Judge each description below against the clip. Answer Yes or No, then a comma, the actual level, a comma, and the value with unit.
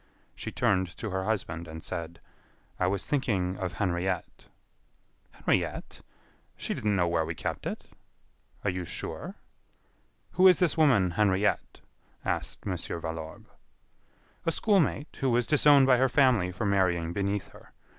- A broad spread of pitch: Yes, wide, 6.2 semitones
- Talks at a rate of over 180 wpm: No, average, 145 wpm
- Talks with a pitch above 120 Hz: No, very low, 95 Hz